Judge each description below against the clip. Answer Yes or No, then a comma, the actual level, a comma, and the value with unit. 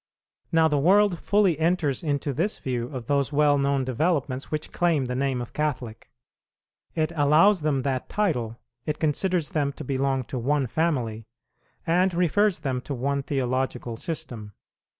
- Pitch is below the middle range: No, medium, 145 Hz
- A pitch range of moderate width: Yes, average, 4.1 semitones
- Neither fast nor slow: Yes, average, 155 wpm